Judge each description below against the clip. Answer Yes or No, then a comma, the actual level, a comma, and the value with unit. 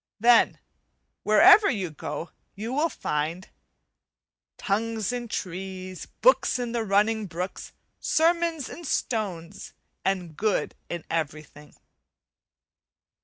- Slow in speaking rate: Yes, slow, 100 wpm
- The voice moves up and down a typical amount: No, wide, 5.8 semitones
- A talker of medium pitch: No, high, 200 Hz